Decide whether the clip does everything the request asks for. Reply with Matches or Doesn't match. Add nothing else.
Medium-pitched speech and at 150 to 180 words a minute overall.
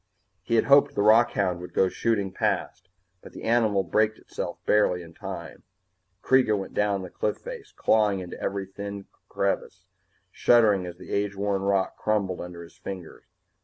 Doesn't match